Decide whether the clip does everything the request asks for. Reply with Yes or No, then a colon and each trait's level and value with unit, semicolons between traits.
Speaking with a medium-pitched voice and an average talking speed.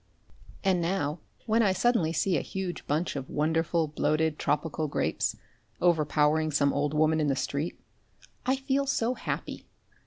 Yes: medium, 160 Hz; average, 150 wpm